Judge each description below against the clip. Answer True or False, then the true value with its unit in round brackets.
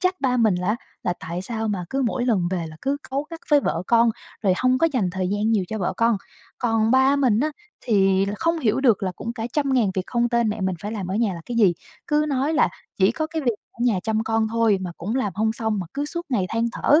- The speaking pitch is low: False (225 Hz)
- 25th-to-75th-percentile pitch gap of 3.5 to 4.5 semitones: False (5.0 semitones)